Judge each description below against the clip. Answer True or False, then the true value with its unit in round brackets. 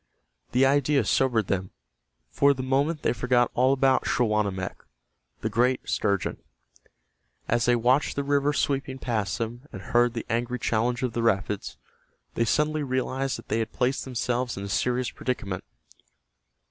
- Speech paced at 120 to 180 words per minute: True (155 wpm)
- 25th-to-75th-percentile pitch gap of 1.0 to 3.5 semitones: True (2.9 semitones)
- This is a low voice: True (125 Hz)